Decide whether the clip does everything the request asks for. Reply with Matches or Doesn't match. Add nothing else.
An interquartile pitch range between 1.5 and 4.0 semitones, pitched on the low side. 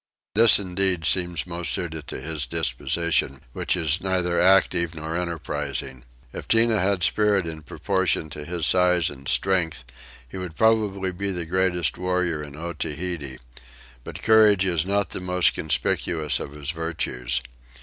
Matches